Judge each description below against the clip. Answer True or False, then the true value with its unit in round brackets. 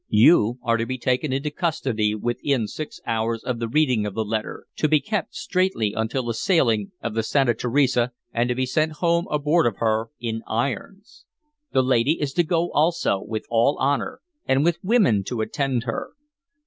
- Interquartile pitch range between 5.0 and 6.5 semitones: True (5.3 semitones)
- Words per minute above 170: True (185 wpm)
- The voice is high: False (130 Hz)